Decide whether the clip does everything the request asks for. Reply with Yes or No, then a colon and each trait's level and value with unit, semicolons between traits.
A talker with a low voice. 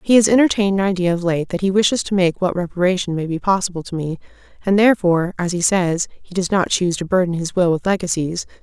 No: medium, 185 Hz